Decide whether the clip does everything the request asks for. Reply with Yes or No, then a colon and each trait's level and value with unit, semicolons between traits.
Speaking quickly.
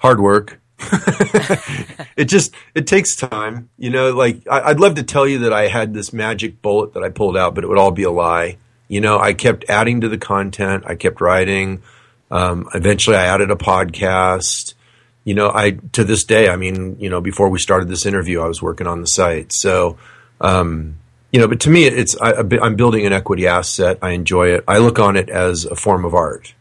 Yes: fast, 220 wpm